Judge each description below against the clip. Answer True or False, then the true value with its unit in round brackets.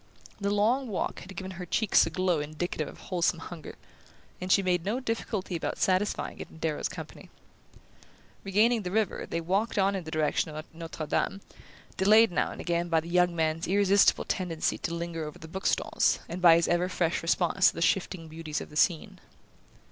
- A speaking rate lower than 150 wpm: False (195 wpm)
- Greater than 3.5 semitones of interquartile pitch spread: False (3.0 semitones)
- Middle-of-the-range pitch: True (180 Hz)